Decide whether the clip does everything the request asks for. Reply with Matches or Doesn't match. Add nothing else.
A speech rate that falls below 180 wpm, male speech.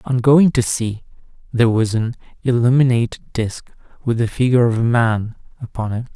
Matches